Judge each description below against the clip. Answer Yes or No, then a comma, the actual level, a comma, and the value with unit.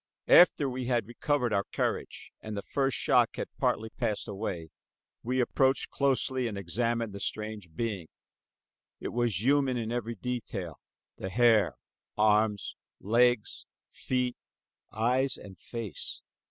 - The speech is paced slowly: Yes, slow, 130 wpm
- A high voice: No, low, 115 Hz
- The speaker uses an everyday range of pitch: Yes, average, 3.3 semitones